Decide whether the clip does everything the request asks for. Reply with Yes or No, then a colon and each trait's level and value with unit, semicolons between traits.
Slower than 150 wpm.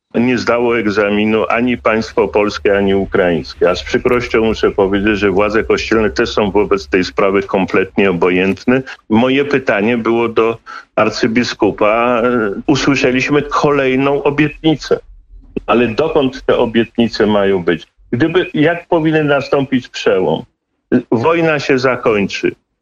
Yes: average, 120 wpm